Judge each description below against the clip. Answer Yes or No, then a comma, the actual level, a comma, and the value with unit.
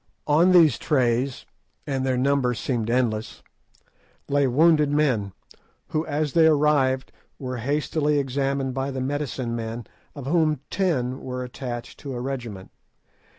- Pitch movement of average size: Yes, average, 3.0 semitones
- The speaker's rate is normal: No, slow, 125 wpm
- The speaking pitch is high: No, low, 135 Hz